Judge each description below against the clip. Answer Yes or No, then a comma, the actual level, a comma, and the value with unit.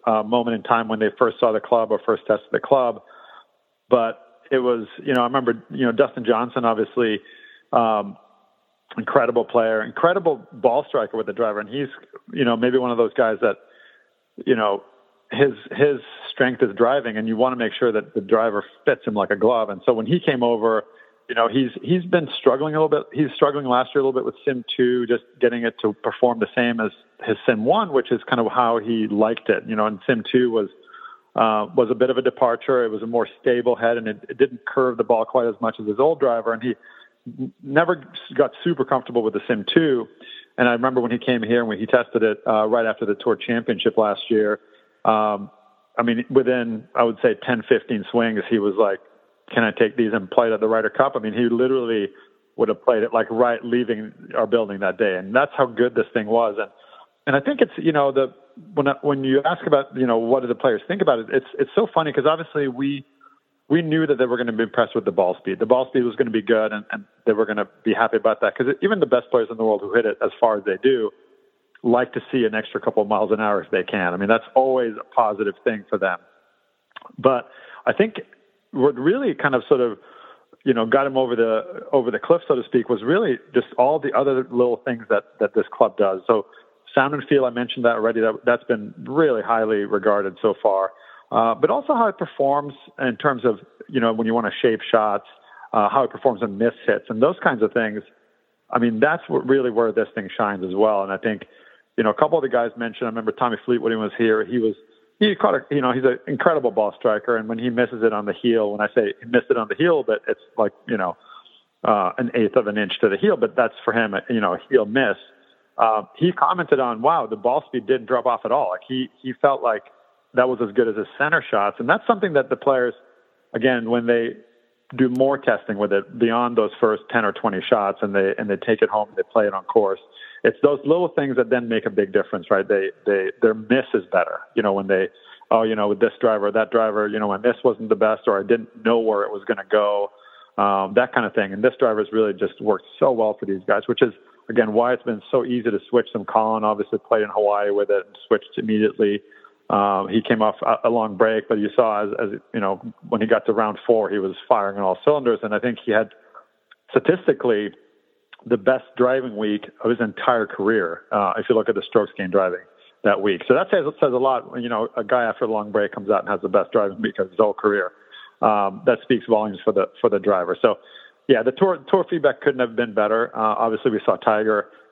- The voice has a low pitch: Yes, low, 120 Hz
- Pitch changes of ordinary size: Yes, average, 3.9 semitones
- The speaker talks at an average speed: No, fast, 250 wpm